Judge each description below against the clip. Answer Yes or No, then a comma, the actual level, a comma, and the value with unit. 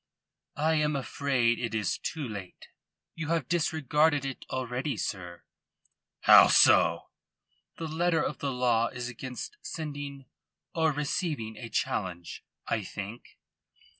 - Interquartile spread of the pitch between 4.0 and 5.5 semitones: Yes, average, 4.8 semitones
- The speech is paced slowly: Yes, slow, 125 wpm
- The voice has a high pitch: No, low, 135 Hz